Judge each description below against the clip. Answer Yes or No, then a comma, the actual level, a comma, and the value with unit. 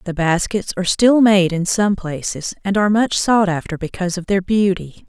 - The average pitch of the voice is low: No, high, 195 Hz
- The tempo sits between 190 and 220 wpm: Yes, average, 200 wpm